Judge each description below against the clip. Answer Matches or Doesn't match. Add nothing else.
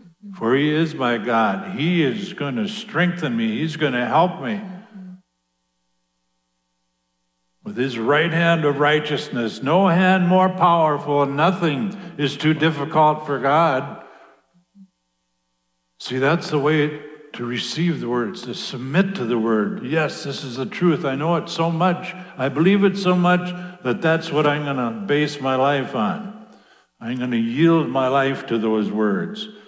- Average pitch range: Doesn't match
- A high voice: Doesn't match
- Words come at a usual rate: Matches